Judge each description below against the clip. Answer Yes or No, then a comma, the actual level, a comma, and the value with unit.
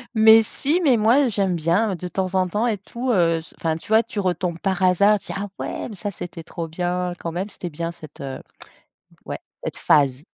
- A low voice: No, medium, 185 Hz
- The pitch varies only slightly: No, average, 4.0 semitones